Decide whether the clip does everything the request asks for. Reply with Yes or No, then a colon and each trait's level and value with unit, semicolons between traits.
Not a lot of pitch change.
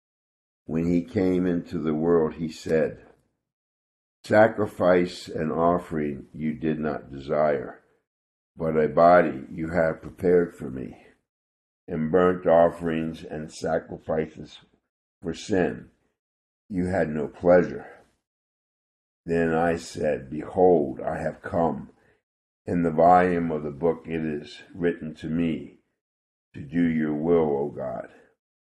Yes: narrow, 2.0 semitones